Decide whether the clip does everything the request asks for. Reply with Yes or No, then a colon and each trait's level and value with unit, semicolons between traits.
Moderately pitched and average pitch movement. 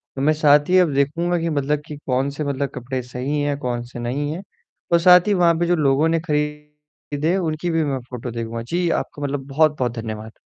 Yes: medium, 145 Hz; average, 3.3 semitones